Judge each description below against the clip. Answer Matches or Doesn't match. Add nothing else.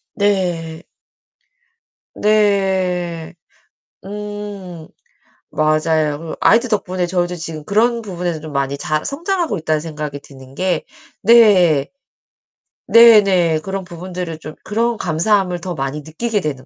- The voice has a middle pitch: Matches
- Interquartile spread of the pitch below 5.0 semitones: Matches